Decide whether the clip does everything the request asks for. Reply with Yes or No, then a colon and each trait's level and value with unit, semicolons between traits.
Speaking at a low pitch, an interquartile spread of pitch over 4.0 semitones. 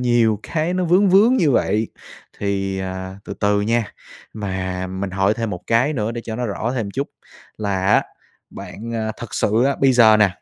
No: low, 110 Hz; average, 3.7 semitones